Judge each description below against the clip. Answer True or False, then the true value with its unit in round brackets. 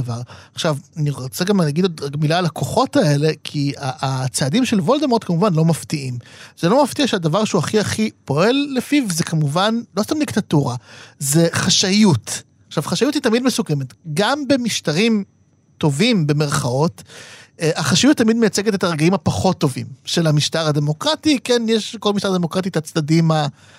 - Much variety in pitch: True (7.0 semitones)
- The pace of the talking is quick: True (155 wpm)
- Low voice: False (165 Hz)